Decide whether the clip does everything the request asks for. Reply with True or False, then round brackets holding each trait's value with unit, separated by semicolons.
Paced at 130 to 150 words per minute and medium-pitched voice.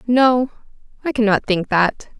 False (135 wpm; 225 Hz)